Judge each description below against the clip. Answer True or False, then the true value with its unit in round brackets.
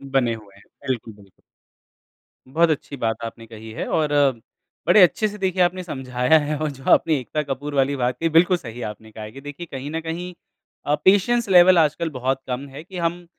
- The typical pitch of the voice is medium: True (145 Hz)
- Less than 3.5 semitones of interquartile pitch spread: False (5.6 semitones)